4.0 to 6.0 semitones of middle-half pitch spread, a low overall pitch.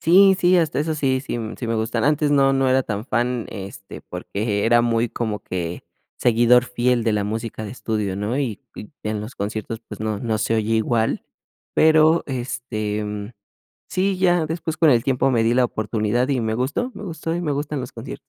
Yes: average, 4.7 semitones; low, 120 Hz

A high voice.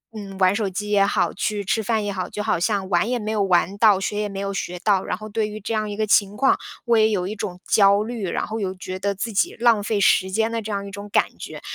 Yes: high, 205 Hz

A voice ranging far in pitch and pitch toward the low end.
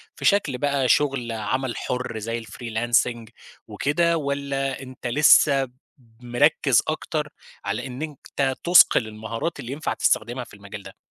No: average, 3.5 semitones; low, 130 Hz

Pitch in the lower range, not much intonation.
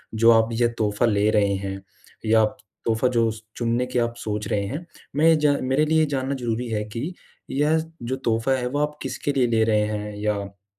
No: low, 115 Hz; average, 3.8 semitones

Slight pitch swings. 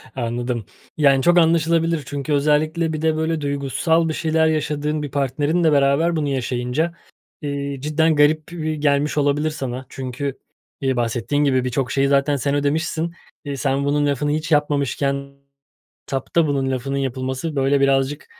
Yes: narrow, 2.3 semitones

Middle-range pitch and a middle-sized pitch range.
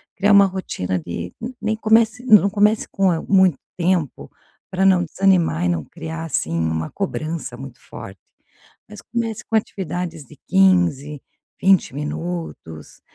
No: medium, 175 Hz; wide, 5.8 semitones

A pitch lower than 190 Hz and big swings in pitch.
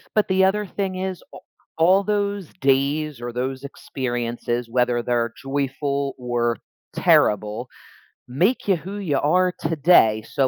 Yes: medium, 140 Hz; wide, 7.2 semitones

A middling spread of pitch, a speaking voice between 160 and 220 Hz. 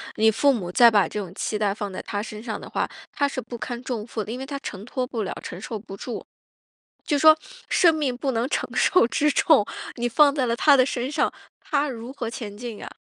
No: average, 4.4 semitones; high, 240 Hz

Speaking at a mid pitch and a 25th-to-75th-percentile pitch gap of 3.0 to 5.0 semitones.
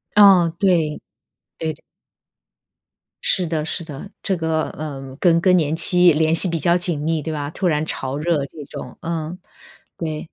No: medium, 160 Hz; narrow, 2.4 semitones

